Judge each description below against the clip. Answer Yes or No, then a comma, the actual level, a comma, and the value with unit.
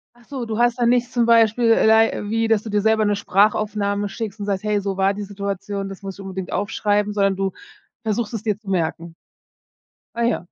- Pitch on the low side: No, high, 205 Hz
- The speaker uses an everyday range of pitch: No, narrow, 2.3 semitones